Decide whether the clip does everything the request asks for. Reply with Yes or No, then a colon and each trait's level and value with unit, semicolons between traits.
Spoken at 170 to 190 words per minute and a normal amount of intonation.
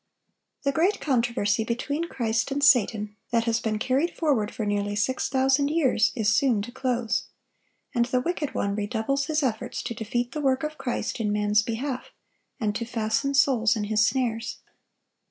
Yes: average, 175 wpm; average, 3.8 semitones